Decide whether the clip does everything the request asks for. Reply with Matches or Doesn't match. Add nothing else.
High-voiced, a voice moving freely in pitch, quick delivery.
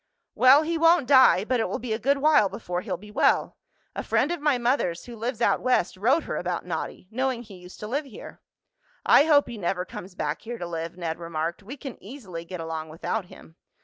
Matches